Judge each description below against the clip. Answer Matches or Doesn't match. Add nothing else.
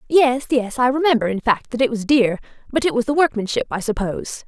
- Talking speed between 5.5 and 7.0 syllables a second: Matches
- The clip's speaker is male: Doesn't match